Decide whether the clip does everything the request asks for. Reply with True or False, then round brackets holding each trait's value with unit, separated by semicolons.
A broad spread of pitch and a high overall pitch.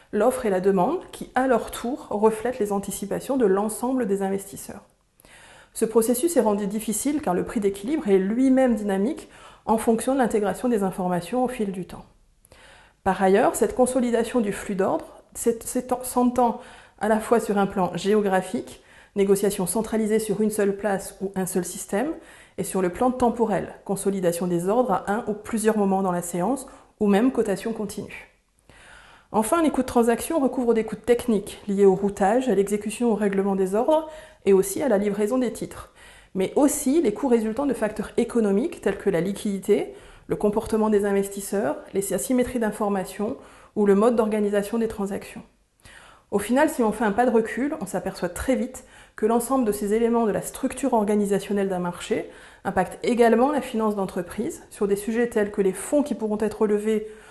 False (3.6 semitones; 215 Hz)